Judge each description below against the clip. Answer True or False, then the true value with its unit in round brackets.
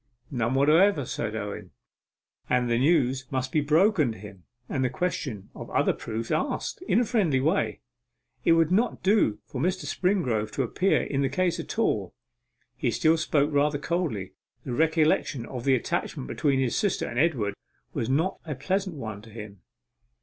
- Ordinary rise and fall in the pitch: False (6.3 semitones)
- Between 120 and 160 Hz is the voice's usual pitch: True (140 Hz)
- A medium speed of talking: True (175 wpm)